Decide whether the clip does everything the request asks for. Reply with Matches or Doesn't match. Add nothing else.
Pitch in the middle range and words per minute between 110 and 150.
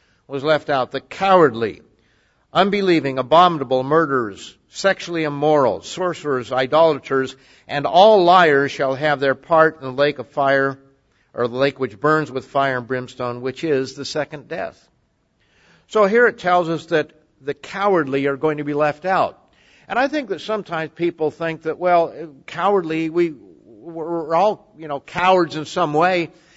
Doesn't match